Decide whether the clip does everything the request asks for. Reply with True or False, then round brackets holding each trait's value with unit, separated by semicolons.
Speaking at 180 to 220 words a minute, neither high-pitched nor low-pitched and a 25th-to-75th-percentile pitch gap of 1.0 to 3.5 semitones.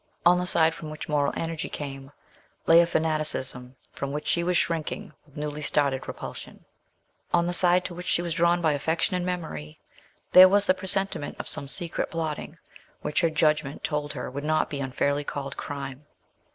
True (185 wpm; 155 Hz; 3.2 semitones)